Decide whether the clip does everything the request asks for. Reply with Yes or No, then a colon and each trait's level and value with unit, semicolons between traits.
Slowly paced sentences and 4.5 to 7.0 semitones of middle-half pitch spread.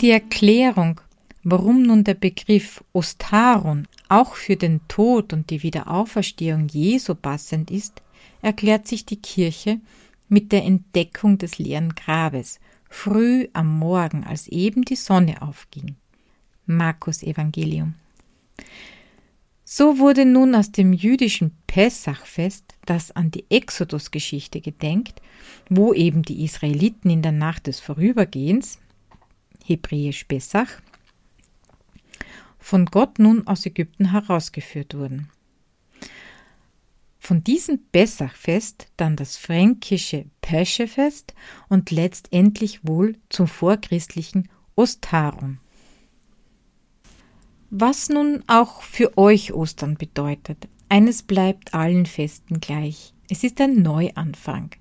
Yes: slow, 105 wpm; average, 5.3 semitones